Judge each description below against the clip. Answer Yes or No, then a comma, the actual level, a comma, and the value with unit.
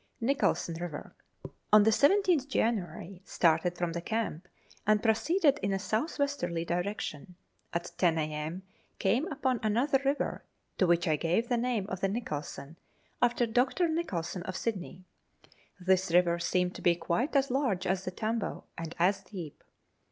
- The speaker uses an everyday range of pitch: No, wide, 5.9 semitones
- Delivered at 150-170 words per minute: Yes, average, 155 wpm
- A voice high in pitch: Yes, high, 195 Hz